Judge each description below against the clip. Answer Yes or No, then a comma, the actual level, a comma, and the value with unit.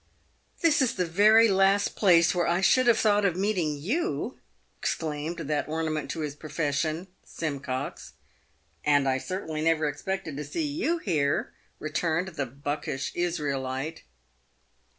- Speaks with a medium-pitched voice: Yes, medium, 165 Hz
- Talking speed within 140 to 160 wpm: Yes, average, 150 wpm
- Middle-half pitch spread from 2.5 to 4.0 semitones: No, average, 4.7 semitones